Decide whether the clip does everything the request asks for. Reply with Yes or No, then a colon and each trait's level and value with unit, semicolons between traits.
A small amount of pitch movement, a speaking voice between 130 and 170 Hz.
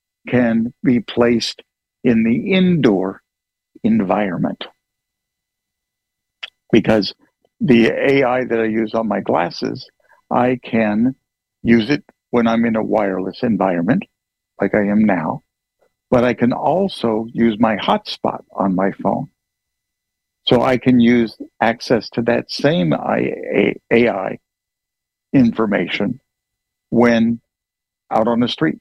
No: narrow, 2.1 semitones; low, 120 Hz